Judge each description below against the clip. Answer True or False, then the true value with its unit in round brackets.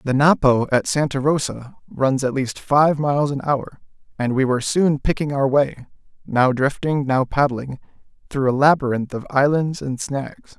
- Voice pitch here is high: False (140 Hz)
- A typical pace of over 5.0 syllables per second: False (4.6 syllables/s)